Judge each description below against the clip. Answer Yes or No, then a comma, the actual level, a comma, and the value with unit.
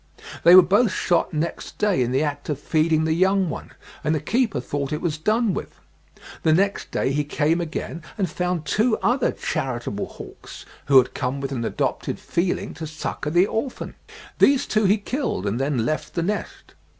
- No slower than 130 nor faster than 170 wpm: No, average, 190 wpm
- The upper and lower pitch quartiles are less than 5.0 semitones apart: No, average, 5.3 semitones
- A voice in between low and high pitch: Yes, medium, 160 Hz